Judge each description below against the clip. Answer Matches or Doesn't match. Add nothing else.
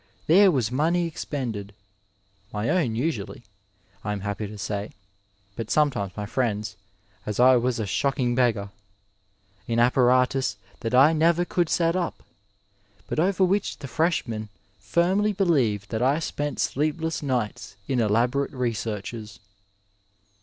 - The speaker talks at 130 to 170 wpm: Matches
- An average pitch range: Doesn't match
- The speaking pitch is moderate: Doesn't match